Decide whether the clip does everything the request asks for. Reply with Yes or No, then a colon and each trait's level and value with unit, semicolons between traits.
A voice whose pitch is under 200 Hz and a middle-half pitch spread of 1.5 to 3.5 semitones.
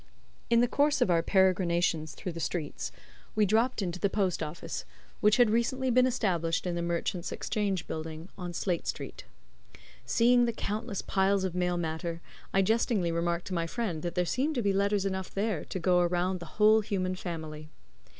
No: medium, 185 Hz; average, 4.0 semitones